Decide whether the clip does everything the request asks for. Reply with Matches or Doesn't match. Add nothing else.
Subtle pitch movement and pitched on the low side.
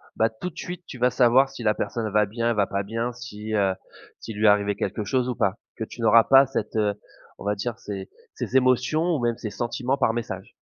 Doesn't match